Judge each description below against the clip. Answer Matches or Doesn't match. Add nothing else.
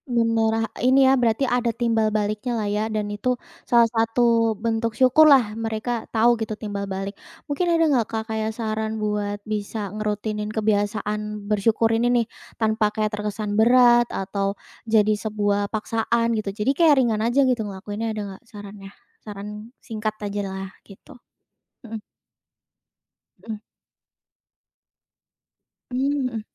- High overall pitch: Matches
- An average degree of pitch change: Doesn't match